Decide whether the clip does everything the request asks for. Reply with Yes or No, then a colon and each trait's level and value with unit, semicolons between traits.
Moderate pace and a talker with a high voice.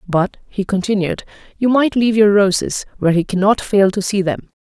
Yes: average, 195 wpm; high, 200 Hz